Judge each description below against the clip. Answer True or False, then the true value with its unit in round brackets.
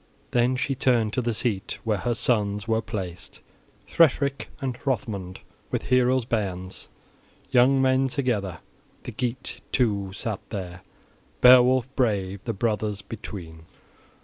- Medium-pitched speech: False (115 Hz)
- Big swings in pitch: False (4.2 semitones)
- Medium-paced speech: False (120 wpm)